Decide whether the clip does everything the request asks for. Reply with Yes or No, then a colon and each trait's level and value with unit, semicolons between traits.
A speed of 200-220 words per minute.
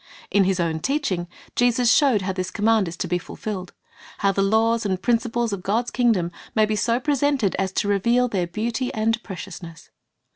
Yes: fast, 205 wpm